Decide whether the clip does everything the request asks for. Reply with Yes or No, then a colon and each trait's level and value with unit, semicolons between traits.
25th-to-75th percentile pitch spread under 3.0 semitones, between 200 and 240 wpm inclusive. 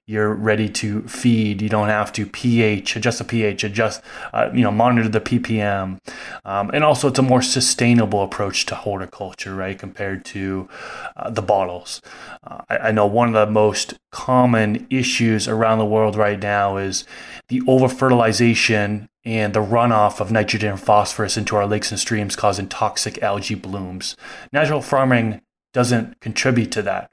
No: narrow, 2.5 semitones; average, 165 wpm